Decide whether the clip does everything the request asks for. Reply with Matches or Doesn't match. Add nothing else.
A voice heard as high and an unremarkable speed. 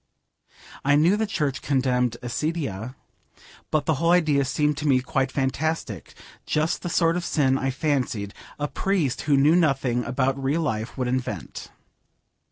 Doesn't match